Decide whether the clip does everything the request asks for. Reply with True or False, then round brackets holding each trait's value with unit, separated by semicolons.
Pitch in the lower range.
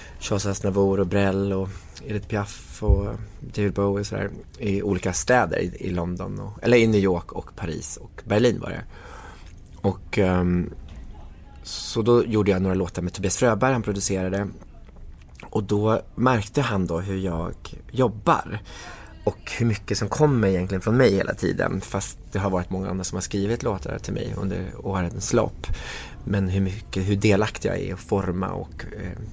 True (100 Hz)